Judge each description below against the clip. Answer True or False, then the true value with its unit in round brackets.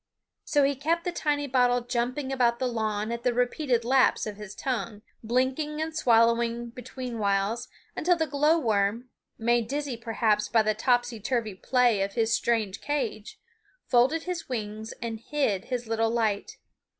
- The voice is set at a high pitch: True (240 Hz)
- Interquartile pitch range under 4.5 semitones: True (3.2 semitones)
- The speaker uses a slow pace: False (160 wpm)